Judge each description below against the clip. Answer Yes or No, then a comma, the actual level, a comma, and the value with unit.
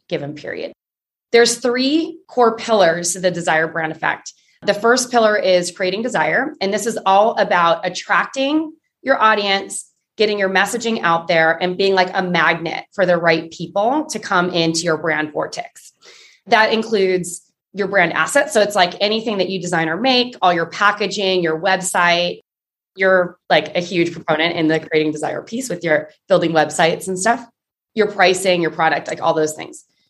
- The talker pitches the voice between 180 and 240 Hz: Yes, medium, 185 Hz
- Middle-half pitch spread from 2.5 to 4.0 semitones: No, average, 4.7 semitones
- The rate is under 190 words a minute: Yes, average, 175 wpm